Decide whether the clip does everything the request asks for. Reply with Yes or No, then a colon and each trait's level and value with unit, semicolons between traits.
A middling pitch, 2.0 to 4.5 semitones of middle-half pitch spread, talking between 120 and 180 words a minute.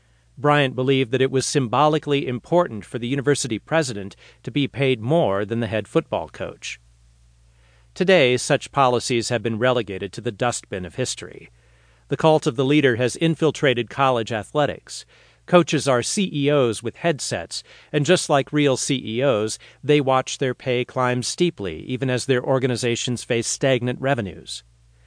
No: low, 125 Hz; average, 3.9 semitones; average, 150 wpm